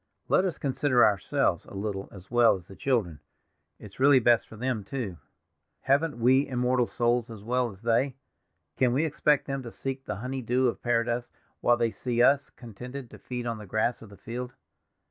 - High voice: No, low, 120 Hz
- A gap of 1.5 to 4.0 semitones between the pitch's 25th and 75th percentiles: Yes, average, 2.8 semitones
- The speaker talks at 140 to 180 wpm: No, average, 195 wpm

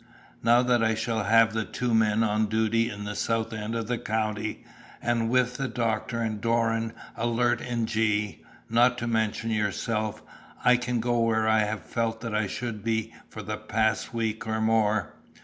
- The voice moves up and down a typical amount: No, narrow, 1.2 semitones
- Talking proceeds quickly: No, average, 185 wpm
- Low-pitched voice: Yes, low, 115 Hz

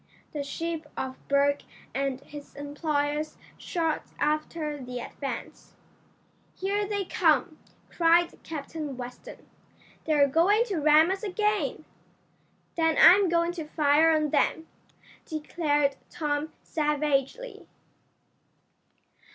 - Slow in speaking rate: Yes, slow, 100 wpm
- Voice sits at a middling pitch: No, very high, 310 Hz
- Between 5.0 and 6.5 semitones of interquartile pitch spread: No, average, 2.8 semitones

